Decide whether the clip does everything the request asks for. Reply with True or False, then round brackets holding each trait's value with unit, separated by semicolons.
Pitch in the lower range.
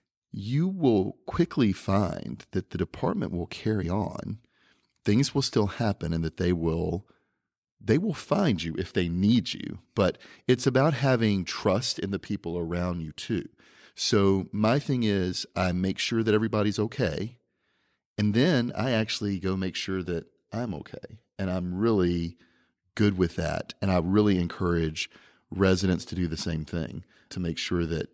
True (95 Hz)